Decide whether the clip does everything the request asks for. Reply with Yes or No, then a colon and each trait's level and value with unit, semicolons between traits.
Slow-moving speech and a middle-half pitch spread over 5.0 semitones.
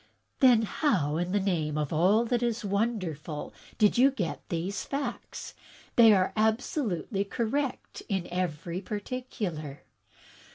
Yes: slow, 125 wpm; wide, 5.5 semitones